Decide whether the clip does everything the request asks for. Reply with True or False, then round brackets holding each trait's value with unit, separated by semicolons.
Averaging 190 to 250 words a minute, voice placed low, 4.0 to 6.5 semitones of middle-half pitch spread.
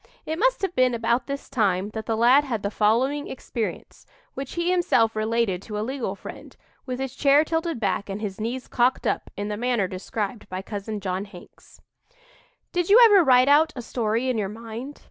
False (200 wpm; 235 Hz; 4.7 semitones)